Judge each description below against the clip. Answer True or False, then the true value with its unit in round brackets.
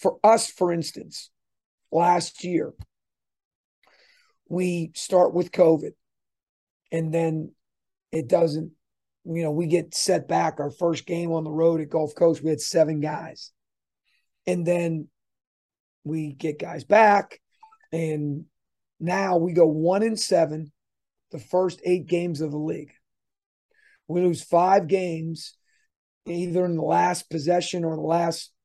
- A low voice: False (170 Hz)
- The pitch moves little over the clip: True (2.1 semitones)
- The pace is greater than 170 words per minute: False (135 wpm)